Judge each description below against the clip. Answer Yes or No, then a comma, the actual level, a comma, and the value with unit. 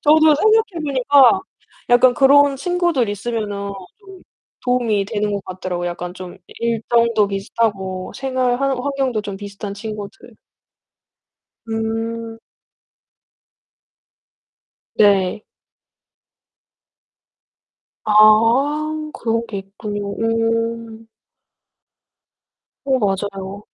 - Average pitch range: Yes, average, 4.4 semitones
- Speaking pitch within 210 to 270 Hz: Yes, high, 225 Hz